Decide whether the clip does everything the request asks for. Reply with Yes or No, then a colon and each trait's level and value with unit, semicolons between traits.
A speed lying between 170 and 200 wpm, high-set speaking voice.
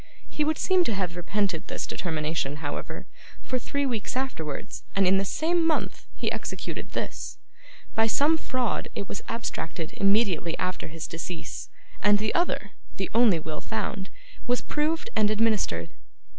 No: average, 155 wpm; high, 205 Hz